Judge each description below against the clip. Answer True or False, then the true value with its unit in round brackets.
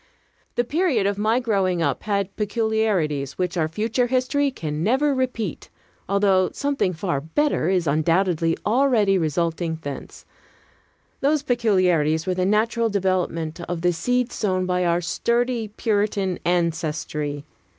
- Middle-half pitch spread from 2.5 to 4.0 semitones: False (5.5 semitones)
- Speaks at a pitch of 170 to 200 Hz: True (190 Hz)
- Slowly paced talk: True (130 wpm)